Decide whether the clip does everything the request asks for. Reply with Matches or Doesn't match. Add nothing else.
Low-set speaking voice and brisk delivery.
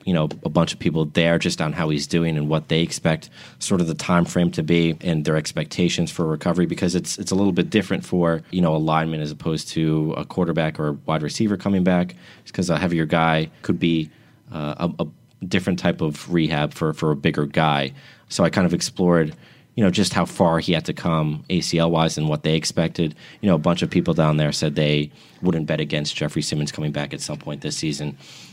Matches